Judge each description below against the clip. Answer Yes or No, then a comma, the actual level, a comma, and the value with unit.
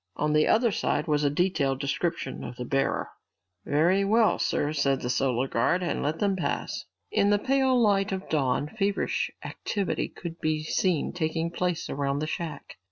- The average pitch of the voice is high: No, medium, 160 Hz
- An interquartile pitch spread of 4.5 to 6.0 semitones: Yes, wide, 5.5 semitones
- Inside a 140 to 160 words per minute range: No, average, 170 wpm